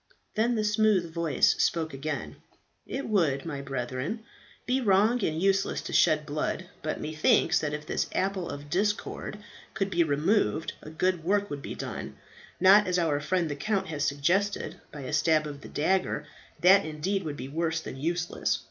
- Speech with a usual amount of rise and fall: Yes, average, 4.6 semitones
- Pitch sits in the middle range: Yes, medium, 165 Hz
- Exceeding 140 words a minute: Yes, average, 175 wpm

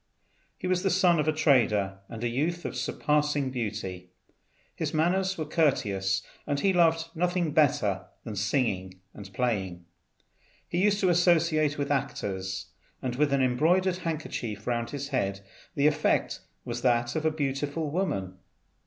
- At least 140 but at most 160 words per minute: Yes, average, 155 wpm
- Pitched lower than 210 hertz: Yes, medium, 140 Hz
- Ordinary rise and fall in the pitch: No, wide, 7.4 semitones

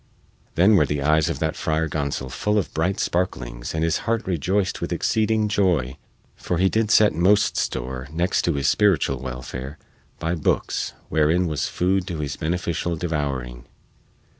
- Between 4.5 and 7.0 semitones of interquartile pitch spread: Yes, average, 5.0 semitones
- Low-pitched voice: Yes, very low, 80 Hz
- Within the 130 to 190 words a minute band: Yes, average, 165 wpm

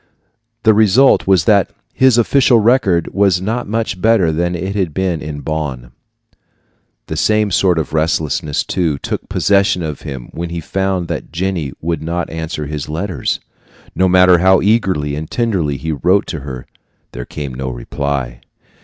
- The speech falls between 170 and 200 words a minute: No, average, 160 wpm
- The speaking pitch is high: No, very low, 85 Hz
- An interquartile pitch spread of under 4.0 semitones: No, average, 4.5 semitones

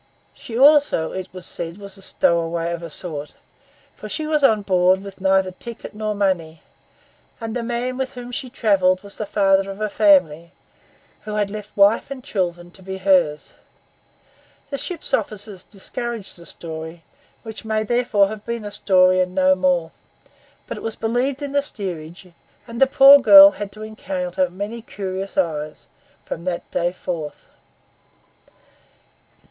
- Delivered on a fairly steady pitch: No, average, 4.2 semitones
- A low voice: No, high, 200 Hz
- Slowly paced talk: No, average, 165 wpm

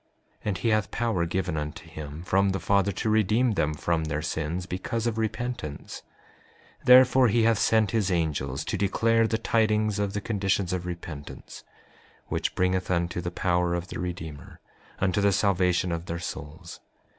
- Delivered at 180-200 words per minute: No, average, 170 wpm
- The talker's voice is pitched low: Yes, very low, 95 Hz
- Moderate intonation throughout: Yes, average, 4.1 semitones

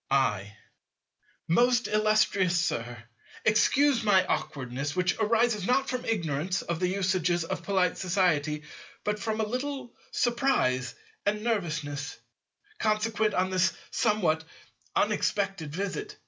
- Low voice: No, high, 190 Hz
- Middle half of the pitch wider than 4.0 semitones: Yes, wide, 5.4 semitones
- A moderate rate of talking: No, slow, 115 wpm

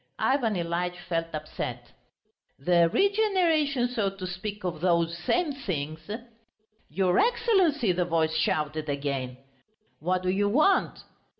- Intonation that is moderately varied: No, wide, 8.5 semitones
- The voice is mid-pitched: Yes, medium, 180 Hz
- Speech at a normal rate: No, slow, 120 wpm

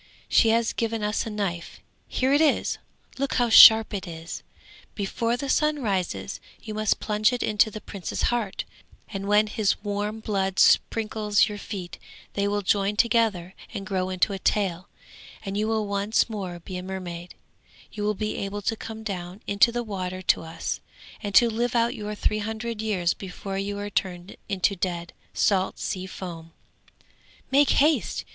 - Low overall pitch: No, high, 205 Hz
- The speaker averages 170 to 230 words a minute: Yes, average, 175 wpm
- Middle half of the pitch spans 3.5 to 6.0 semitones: No, average, 2.7 semitones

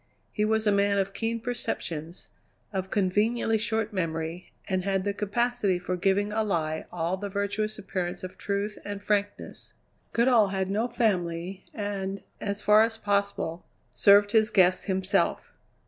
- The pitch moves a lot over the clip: No, narrow, 2.4 semitones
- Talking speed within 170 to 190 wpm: No, average, 150 wpm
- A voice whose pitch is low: No, high, 200 Hz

